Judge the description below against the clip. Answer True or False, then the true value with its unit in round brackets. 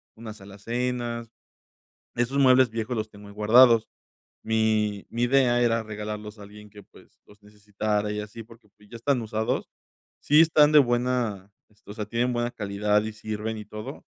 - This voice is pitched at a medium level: False (110 Hz)